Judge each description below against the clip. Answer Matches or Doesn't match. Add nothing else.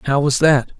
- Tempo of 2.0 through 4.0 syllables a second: Doesn't match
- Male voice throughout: Matches